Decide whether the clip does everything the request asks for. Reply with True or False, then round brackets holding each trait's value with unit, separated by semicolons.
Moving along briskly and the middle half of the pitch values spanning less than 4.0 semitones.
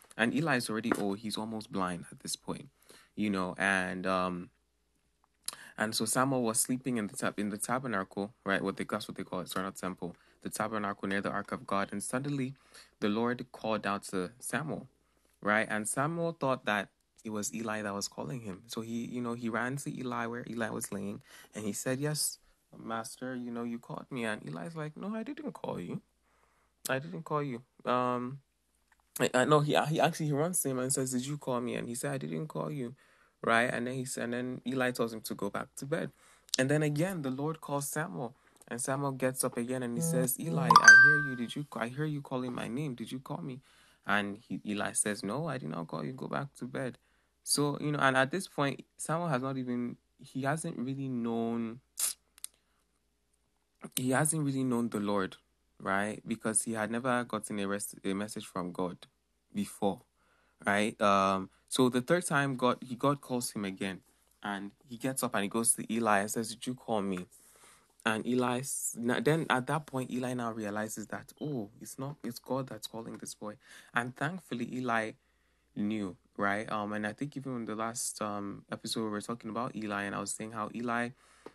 False (210 wpm; 4.4 semitones)